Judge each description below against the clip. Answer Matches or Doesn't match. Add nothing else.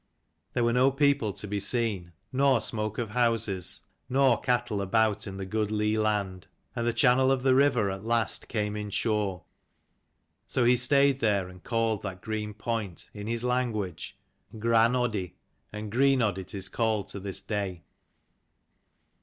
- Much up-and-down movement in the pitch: Doesn't match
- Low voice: Matches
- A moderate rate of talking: Matches